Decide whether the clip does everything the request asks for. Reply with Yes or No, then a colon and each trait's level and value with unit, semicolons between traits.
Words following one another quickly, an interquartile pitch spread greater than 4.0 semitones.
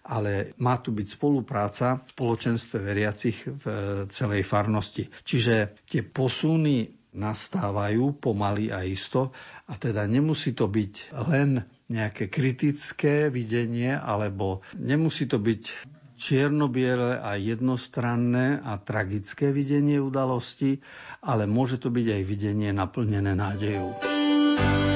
No: slow, 110 wpm; average, 4.5 semitones